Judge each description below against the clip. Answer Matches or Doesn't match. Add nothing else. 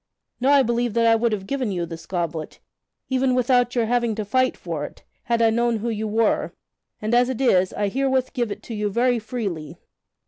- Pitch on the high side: Matches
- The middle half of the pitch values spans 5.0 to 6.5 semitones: Doesn't match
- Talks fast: Matches